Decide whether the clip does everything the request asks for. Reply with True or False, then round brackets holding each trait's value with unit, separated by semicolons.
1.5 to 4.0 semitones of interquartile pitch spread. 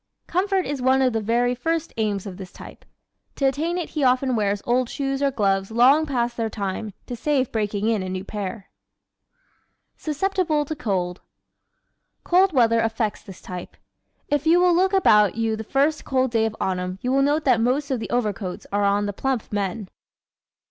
False (5.5 semitones)